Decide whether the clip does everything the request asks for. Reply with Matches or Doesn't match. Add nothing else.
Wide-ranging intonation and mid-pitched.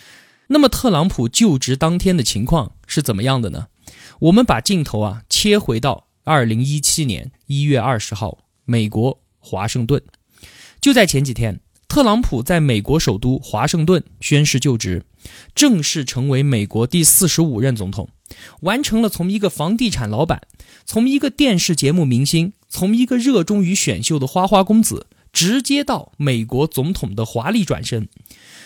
Matches